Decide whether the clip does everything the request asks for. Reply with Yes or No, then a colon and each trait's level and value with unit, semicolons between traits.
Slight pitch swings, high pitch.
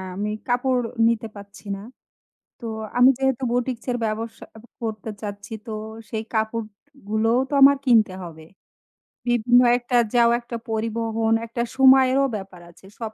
Yes: narrow, 2.2 semitones; high, 230 Hz